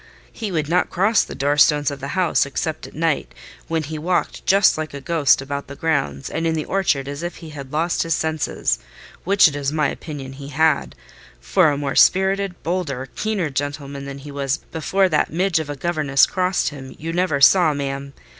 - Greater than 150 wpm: Yes, average, 200 wpm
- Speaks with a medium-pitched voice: Yes, medium, 150 Hz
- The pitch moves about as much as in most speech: Yes, average, 3.5 semitones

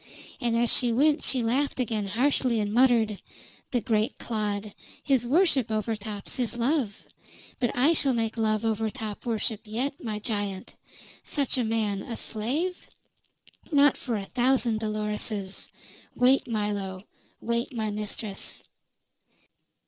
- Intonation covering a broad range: No, average, 3.1 semitones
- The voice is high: Yes, high, 225 Hz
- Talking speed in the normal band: No, slow, 130 wpm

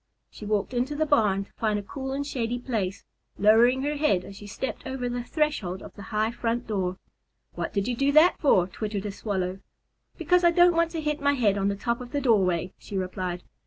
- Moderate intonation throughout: No, wide, 5.8 semitones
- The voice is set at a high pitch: Yes, high, 230 Hz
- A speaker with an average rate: No, fast, 225 wpm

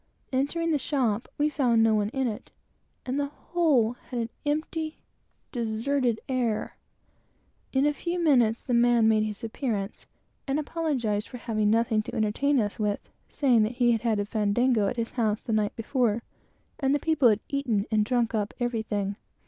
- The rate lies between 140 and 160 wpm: No, average, 175 wpm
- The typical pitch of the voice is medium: No, high, 235 Hz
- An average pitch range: Yes, average, 4.0 semitones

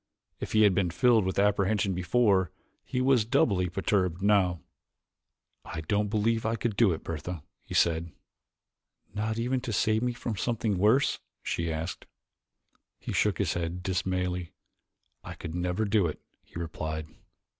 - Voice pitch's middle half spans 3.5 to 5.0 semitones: Yes, average, 3.9 semitones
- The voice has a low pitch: Yes, very low, 95 Hz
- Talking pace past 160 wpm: No, average, 155 wpm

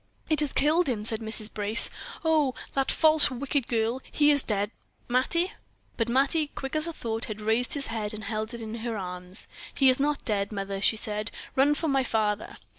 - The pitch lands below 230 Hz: No, high, 235 Hz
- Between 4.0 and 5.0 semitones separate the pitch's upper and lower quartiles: Yes, average, 4.7 semitones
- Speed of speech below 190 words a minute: No, average, 195 wpm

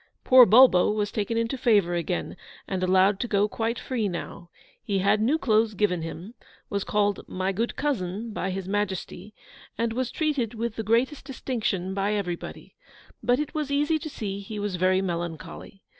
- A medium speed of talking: Yes, average, 175 wpm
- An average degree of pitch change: Yes, average, 3.7 semitones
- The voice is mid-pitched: No, high, 210 Hz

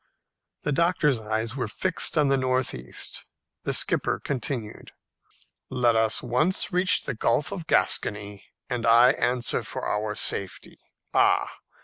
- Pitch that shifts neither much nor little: Yes, average, 4.2 semitones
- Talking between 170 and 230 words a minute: No, slow, 135 wpm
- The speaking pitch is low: Yes, low, 125 Hz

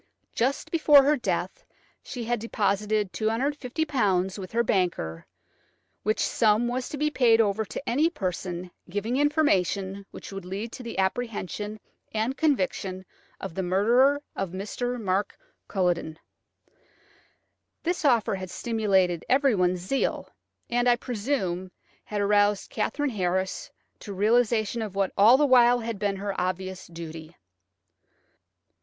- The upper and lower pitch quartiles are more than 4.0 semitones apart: Yes, average, 4.6 semitones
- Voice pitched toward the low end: No, high, 210 Hz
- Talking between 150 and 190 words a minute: No, slow, 135 wpm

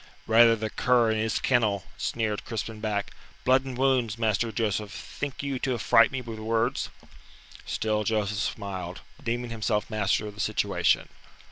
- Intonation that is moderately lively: No, narrow, 2.1 semitones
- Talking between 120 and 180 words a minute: Yes, average, 155 wpm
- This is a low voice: Yes, low, 110 Hz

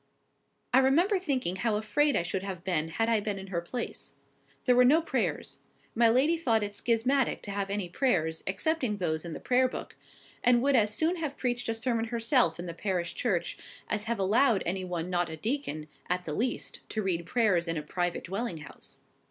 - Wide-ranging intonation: Yes, wide, 5.9 semitones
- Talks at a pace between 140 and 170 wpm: No, fast, 205 wpm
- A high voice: Yes, high, 215 Hz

